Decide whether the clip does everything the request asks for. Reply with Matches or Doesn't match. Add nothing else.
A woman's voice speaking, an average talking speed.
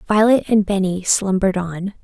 Matches